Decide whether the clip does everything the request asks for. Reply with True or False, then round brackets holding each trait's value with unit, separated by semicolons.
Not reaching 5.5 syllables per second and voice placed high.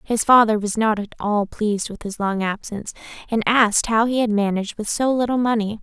False (5.7 syllables/s; 220 Hz)